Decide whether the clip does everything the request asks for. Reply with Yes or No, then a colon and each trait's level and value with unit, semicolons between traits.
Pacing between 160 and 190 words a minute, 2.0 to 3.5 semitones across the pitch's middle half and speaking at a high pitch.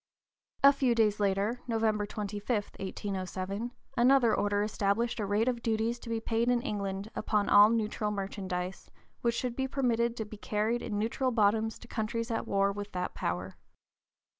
Yes: average, 165 wpm; narrow, 2.5 semitones; high, 215 Hz